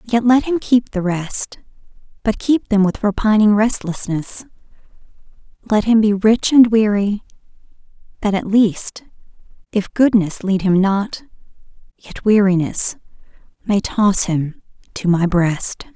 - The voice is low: No, high, 205 Hz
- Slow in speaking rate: Yes, slow, 130 wpm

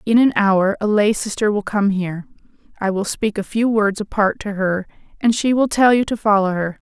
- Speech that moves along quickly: Yes, fast, 225 wpm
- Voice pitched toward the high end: Yes, high, 205 Hz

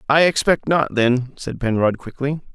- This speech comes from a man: Yes, male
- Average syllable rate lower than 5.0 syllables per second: Yes, 4.5 syllables/s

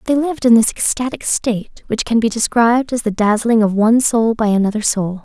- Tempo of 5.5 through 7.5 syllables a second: Yes, 5.8 syllables/s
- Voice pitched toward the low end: No, high, 230 Hz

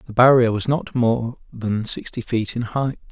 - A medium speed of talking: Yes, average, 190 wpm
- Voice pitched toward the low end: Yes, low, 120 Hz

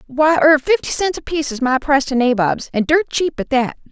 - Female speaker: Yes, female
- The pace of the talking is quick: Yes, fast, 215 wpm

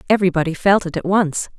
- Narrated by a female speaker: Yes, female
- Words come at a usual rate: Yes, average, 190 wpm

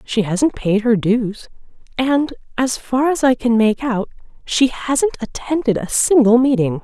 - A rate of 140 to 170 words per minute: Yes, average, 165 wpm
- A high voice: Yes, high, 240 Hz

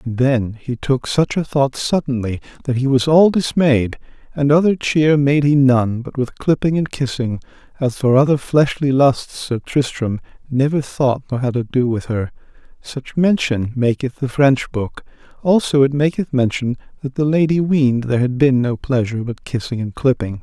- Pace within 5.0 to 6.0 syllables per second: No, 4.7 syllables/s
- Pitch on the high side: No, low, 135 Hz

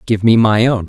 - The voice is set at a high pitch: No, low, 110 Hz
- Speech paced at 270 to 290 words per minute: Yes, fast, 275 wpm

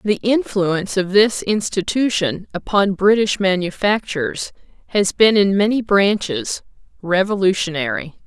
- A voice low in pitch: No, high, 200 Hz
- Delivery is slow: Yes, slow, 100 wpm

